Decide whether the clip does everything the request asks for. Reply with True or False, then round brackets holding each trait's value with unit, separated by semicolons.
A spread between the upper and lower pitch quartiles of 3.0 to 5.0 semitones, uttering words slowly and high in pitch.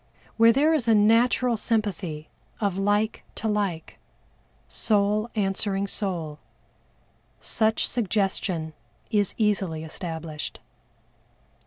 True (3.8 semitones; 95 wpm; 205 Hz)